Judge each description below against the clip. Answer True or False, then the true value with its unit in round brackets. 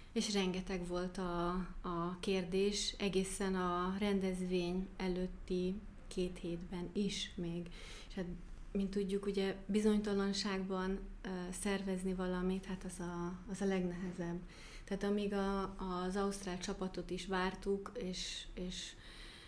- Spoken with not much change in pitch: True (1.6 semitones)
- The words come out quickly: False (120 wpm)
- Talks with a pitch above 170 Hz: True (185 Hz)